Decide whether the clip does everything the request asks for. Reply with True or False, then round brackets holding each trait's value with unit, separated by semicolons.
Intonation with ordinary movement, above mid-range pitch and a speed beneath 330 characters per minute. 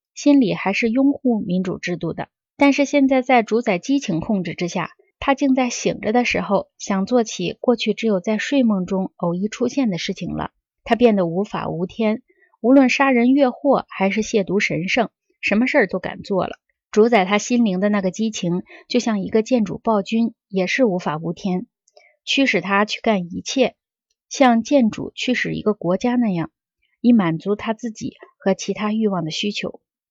True (4.6 semitones; 220 Hz; 265 characters per minute)